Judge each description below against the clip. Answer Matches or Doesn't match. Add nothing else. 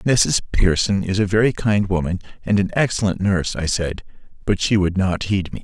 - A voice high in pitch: Doesn't match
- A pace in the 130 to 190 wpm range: Doesn't match